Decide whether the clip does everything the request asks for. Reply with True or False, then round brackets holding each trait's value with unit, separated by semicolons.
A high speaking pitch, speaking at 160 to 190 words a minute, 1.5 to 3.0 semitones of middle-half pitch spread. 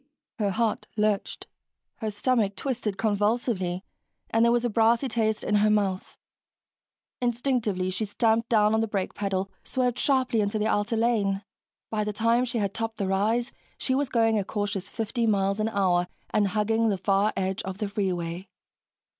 True (215 Hz; 170 wpm; 2.6 semitones)